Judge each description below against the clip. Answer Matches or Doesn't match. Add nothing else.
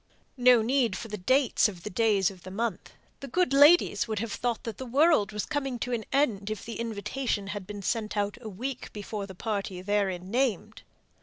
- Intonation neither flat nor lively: Matches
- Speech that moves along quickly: Matches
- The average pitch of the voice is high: Matches